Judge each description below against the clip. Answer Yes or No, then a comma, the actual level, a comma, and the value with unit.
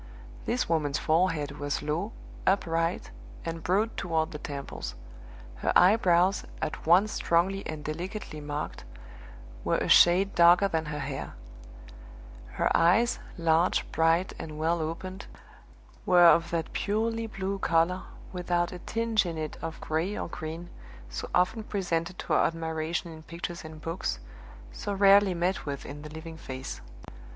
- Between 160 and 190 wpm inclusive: No, average, 145 wpm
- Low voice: No, medium, 170 Hz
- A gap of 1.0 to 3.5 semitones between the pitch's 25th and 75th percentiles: Yes, average, 2.9 semitones